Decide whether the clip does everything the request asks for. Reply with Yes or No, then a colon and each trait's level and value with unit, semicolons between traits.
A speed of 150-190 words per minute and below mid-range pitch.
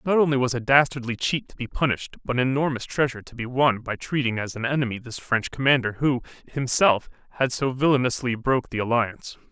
No: average, 200 wpm; low, 125 Hz